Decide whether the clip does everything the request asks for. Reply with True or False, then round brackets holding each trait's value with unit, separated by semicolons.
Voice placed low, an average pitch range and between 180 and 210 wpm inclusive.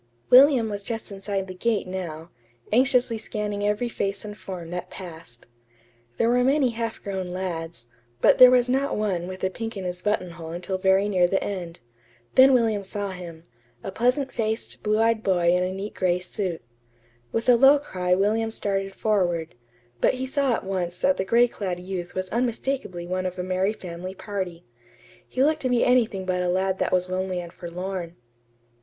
False (195 Hz; 3.9 semitones; 185 wpm)